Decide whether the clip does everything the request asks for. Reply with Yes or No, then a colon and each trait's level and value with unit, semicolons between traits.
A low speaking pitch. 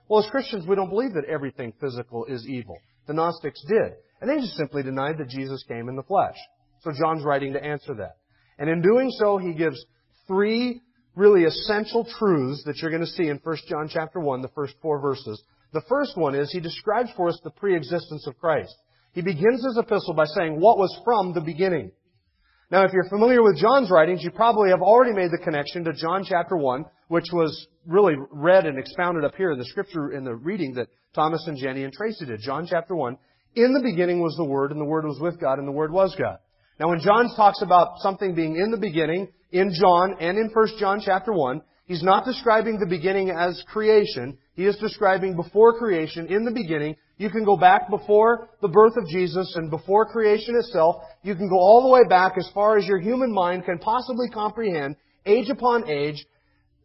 No: medium, 175 Hz